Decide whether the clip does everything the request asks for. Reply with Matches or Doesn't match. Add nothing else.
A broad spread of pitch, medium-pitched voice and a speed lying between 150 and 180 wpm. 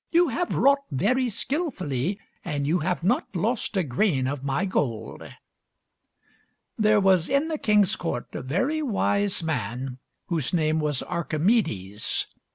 Doesn't match